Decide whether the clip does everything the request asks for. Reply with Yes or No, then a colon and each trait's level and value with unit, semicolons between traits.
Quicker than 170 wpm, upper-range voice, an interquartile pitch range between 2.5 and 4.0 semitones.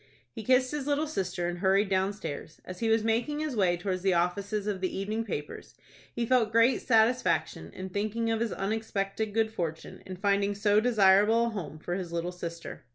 Yes: average, 195 wpm; high, 205 Hz; average, 3.4 semitones